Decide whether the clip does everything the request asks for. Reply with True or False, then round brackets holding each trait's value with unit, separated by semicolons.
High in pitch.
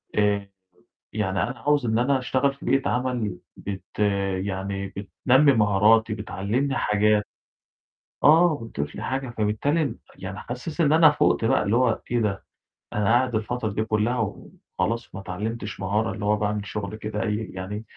False (110 Hz)